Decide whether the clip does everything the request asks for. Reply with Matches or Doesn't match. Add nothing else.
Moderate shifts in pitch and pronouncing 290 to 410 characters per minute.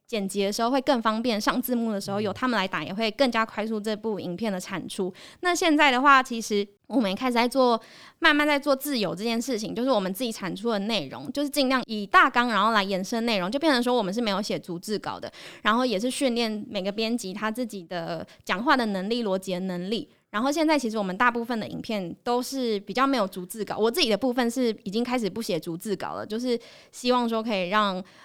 Matches